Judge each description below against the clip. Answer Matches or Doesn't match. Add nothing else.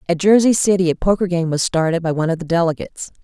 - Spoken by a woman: Matches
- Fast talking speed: Matches